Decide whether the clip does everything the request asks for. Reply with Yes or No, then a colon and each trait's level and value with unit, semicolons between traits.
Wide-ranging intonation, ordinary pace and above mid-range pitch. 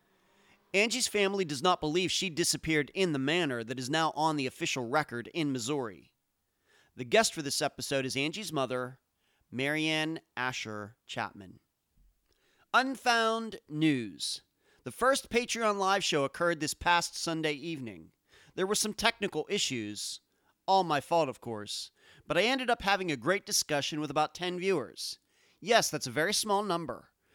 No: wide, 6.2 semitones; average, 155 wpm; medium, 160 Hz